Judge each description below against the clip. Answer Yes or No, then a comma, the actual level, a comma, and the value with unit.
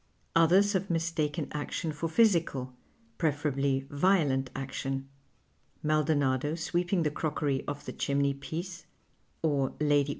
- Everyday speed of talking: No, slow, 125 wpm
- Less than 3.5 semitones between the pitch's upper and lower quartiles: Yes, average, 3.1 semitones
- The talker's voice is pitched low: No, medium, 150 Hz